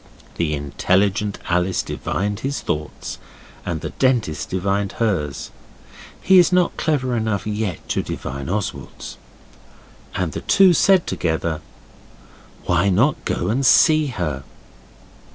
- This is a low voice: Yes, low, 100 Hz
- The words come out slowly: Yes, slow, 120 wpm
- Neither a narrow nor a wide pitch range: No, wide, 7.1 semitones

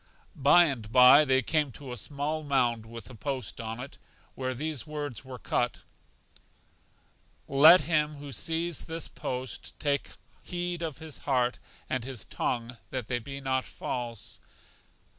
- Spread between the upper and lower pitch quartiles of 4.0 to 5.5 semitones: No, average, 3.5 semitones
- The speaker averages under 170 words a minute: Yes, average, 150 wpm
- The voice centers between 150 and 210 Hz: No, low, 135 Hz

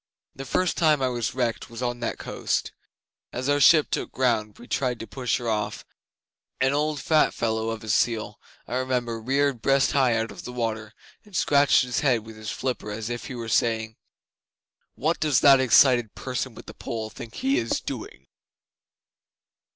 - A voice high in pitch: No, low, 120 Hz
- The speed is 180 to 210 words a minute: Yes, average, 190 wpm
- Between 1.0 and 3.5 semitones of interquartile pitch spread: Yes, average, 3.2 semitones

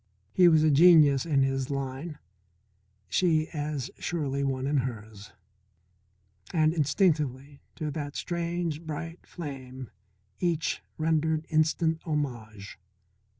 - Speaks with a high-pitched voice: No, medium, 150 Hz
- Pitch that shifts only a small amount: No, average, 3.2 semitones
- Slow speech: Yes, slow, 105 wpm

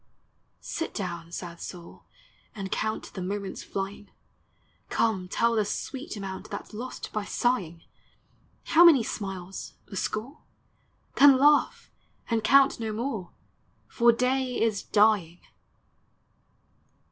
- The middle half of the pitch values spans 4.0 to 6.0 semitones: Yes, average, 4.8 semitones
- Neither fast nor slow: No, slow, 125 wpm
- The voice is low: No, high, 215 Hz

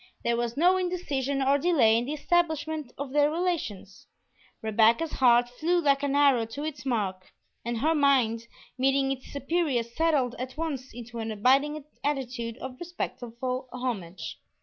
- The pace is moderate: Yes, average, 150 wpm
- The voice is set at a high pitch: Yes, very high, 265 Hz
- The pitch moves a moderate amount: Yes, average, 4.1 semitones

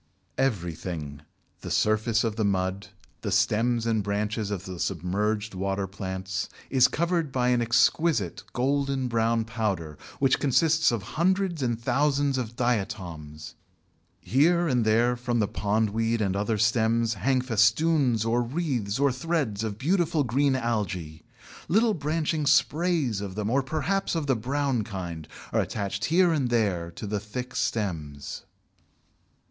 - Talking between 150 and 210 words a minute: No, average, 140 wpm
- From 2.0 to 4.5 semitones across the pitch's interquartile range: No, wide, 5.4 semitones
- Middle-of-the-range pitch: No, low, 115 Hz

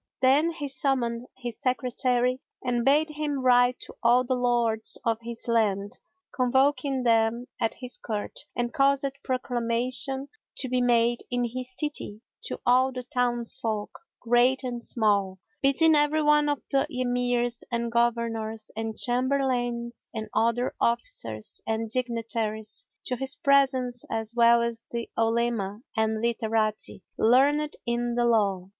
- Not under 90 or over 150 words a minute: Yes, average, 140 wpm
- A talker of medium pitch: No, high, 240 Hz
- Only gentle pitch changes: Yes, narrow, 2.2 semitones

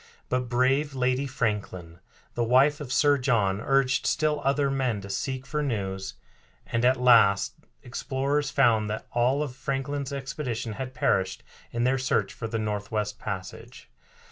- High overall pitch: No, low, 125 Hz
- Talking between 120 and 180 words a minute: Yes, average, 150 wpm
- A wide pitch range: No, average, 4.2 semitones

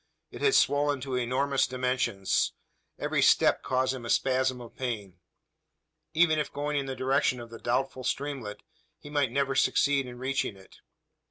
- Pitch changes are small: Yes, narrow, 2.3 semitones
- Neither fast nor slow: Yes, average, 165 wpm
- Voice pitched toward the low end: Yes, low, 130 Hz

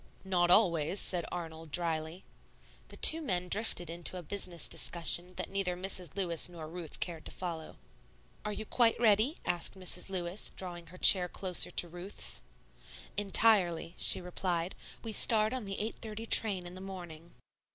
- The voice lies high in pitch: No, medium, 180 Hz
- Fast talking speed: No, average, 160 wpm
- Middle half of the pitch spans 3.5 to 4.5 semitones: No, average, 2.7 semitones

